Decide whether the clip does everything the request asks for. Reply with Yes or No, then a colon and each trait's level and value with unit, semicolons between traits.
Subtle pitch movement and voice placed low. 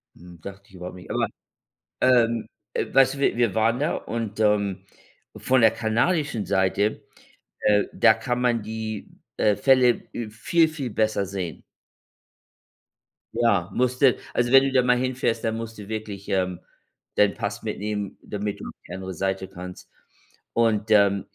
No: average, 3.4 semitones; low, 110 Hz